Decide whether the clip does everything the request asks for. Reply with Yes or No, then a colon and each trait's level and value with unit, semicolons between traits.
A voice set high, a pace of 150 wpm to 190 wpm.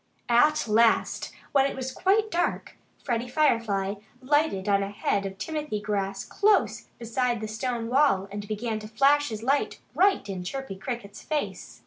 Yes: high, 235 Hz; average, 160 wpm